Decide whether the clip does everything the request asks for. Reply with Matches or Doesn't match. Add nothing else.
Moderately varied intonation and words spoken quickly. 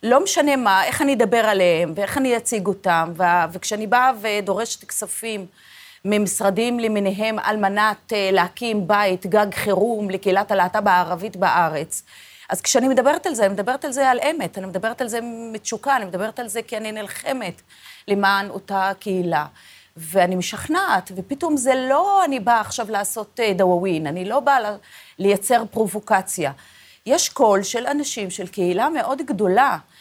Matches